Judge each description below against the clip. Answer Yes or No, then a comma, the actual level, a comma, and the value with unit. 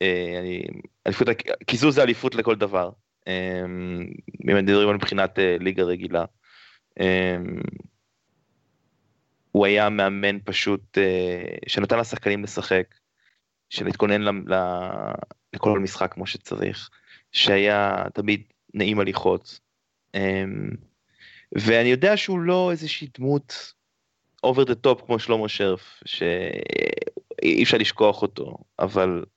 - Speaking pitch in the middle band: No, low, 100 Hz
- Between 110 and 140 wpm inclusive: No, slow, 100 wpm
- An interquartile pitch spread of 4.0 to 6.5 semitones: Yes, average, 4.5 semitones